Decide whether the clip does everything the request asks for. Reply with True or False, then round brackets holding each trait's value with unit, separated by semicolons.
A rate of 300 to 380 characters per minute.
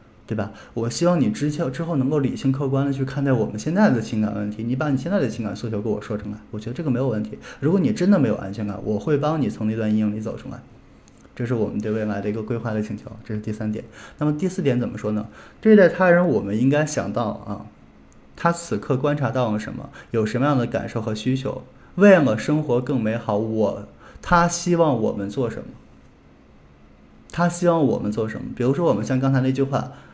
True (340 characters per minute)